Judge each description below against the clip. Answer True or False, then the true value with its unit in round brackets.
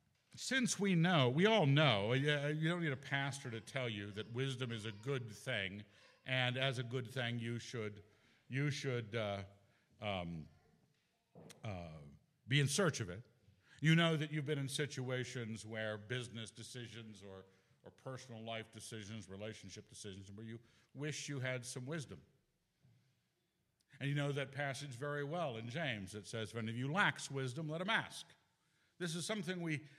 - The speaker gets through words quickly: False (165 wpm)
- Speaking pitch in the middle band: False (125 Hz)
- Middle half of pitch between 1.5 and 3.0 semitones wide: False (4.8 semitones)